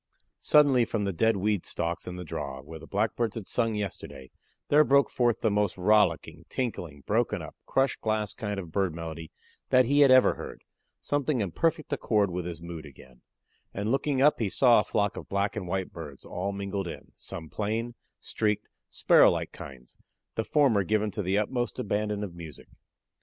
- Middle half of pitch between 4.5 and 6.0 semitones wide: Yes, average, 5.1 semitones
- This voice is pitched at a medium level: No, low, 105 Hz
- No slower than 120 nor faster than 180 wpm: No, average, 190 wpm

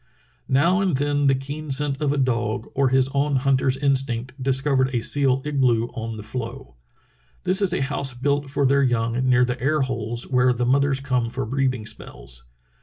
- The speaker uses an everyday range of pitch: No, narrow, 2.3 semitones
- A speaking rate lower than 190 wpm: No, average, 195 wpm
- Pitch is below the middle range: Yes, low, 130 Hz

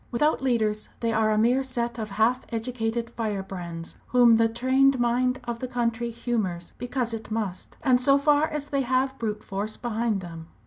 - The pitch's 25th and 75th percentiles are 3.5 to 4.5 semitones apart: No, average, 2.7 semitones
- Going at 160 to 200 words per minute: Yes, average, 180 wpm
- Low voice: No, high, 235 Hz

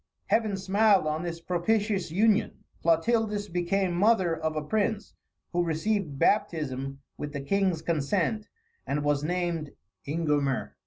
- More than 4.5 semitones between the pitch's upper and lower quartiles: Yes, average, 4.9 semitones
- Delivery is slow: Yes, slow, 125 wpm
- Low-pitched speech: No, medium, 175 Hz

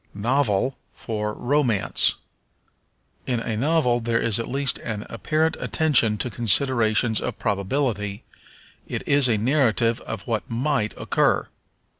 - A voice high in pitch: No, low, 115 Hz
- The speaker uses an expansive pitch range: No, average, 4.0 semitones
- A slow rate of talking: Yes, slow, 125 wpm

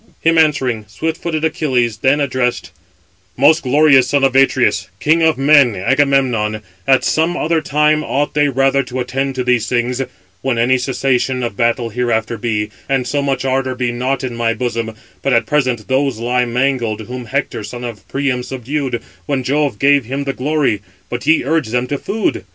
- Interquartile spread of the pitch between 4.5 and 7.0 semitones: No, average, 2.9 semitones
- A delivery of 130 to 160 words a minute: No, average, 180 wpm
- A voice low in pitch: Yes, low, 130 Hz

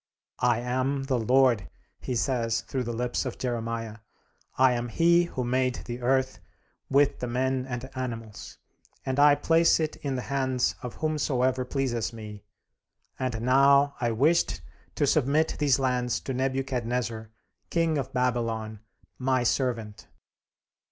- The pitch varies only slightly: Yes, narrow, 2.2 semitones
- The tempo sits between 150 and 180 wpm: No, average, 140 wpm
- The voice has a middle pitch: No, low, 130 Hz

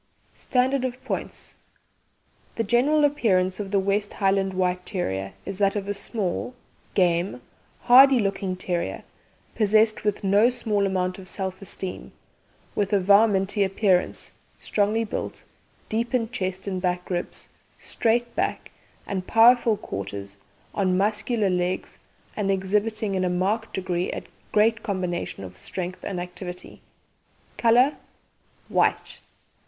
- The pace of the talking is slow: Yes, slow, 130 wpm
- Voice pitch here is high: Yes, high, 195 Hz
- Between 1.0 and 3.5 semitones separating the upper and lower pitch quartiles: Yes, average, 3.2 semitones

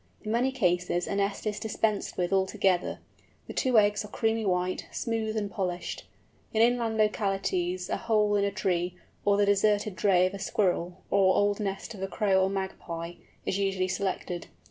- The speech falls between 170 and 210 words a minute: Yes, average, 180 wpm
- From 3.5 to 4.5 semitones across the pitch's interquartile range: No, narrow, 2.4 semitones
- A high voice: Yes, high, 200 Hz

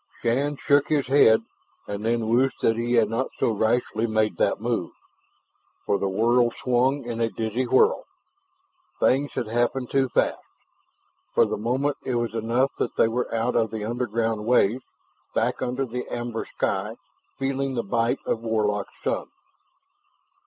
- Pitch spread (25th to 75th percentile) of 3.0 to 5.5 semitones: No, narrow, 2.4 semitones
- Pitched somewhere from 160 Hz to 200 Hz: No, low, 120 Hz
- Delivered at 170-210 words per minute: No, average, 160 wpm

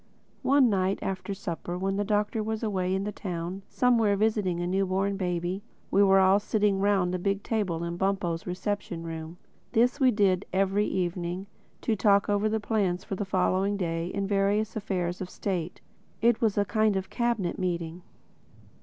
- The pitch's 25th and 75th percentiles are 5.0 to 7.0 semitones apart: No, narrow, 2.4 semitones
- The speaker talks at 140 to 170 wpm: No, average, 180 wpm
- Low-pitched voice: No, high, 195 Hz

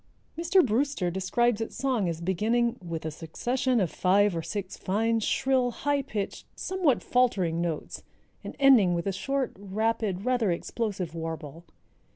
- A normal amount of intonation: No, wide, 6.0 semitones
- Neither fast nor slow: Yes, average, 150 wpm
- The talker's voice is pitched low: No, high, 210 Hz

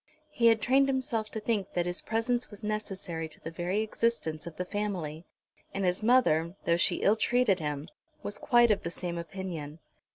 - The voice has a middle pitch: No, high, 195 Hz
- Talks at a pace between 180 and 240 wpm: Yes, average, 190 wpm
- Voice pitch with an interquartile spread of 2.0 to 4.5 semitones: No, average, 5.0 semitones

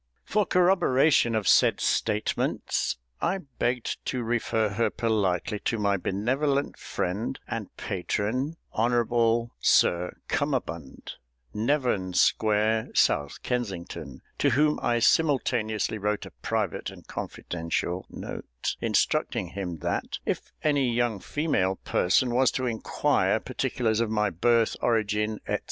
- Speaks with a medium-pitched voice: No, low, 115 Hz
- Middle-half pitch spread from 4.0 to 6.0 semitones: No, average, 3.4 semitones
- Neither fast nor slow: No, slow, 120 wpm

